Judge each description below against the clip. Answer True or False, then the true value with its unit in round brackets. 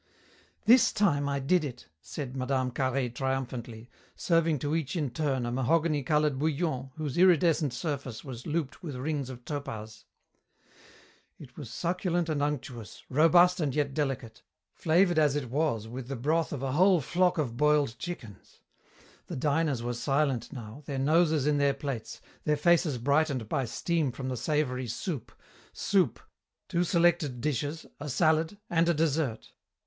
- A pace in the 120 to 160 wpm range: True (155 wpm)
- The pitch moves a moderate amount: True (4.0 semitones)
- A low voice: False (145 Hz)